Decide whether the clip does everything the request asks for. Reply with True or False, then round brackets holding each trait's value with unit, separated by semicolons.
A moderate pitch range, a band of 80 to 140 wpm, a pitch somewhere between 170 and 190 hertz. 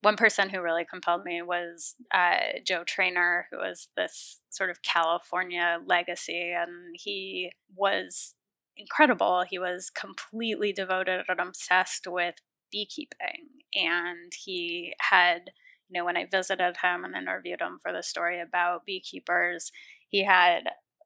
True (3.3 semitones; 135 wpm; 185 Hz)